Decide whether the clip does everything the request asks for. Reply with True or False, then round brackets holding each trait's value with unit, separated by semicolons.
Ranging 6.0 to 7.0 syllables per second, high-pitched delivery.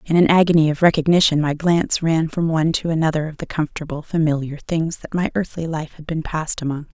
False (6.4 syllables/s; 160 Hz)